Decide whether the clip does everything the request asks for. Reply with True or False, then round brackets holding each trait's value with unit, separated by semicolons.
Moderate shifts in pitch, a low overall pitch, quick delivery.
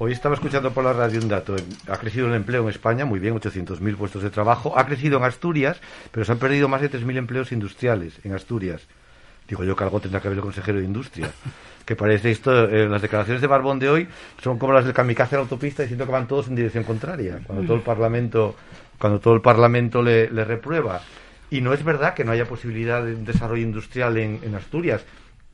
True (3.5 semitones; 115 Hz; 230 wpm)